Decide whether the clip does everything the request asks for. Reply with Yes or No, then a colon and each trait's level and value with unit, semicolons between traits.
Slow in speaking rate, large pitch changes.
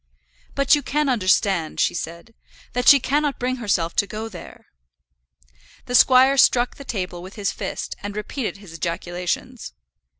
No: average, 155 wpm; wide, 6.1 semitones